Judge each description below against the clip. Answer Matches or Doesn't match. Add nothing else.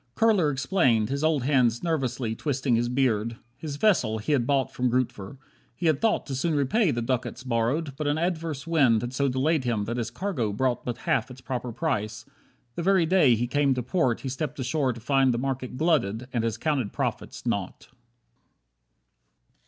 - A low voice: Matches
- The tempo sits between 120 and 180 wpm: Doesn't match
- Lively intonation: Doesn't match